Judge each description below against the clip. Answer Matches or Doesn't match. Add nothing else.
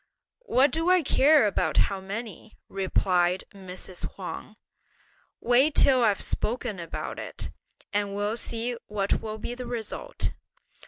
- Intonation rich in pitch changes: Doesn't match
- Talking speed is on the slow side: Matches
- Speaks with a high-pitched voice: Matches